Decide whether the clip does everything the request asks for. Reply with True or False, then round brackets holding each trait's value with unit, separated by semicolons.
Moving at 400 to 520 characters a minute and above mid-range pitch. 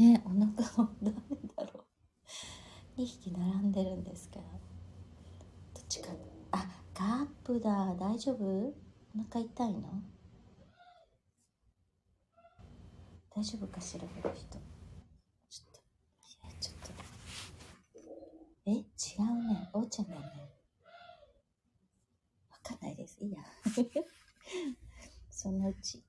False (190 characters per minute; 200 Hz)